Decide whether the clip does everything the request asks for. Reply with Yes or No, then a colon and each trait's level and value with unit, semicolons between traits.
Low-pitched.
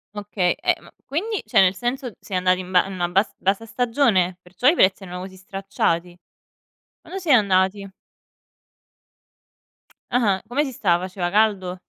No: high, 195 Hz